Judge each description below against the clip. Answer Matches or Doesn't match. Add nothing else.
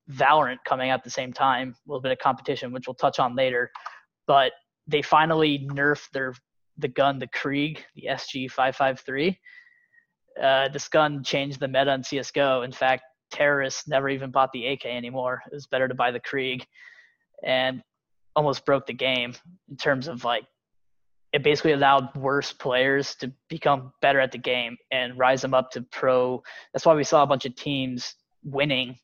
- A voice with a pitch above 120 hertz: Matches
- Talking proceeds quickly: Doesn't match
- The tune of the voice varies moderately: Doesn't match